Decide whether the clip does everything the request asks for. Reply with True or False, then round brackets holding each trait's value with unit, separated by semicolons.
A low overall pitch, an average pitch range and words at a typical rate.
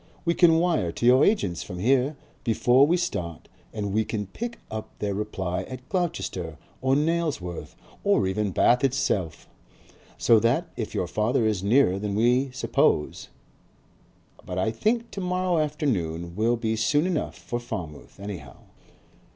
False (115 Hz; 7.6 semitones; 150 wpm)